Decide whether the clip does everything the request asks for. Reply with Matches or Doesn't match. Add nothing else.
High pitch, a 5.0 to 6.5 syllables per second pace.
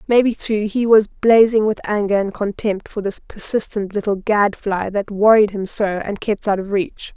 Doesn't match